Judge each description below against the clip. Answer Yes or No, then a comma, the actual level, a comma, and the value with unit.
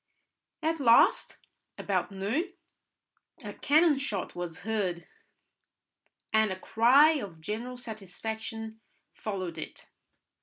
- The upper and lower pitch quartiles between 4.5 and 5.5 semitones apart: Yes, average, 4.8 semitones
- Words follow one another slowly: Yes, slow, 100 wpm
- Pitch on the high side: Yes, high, 220 Hz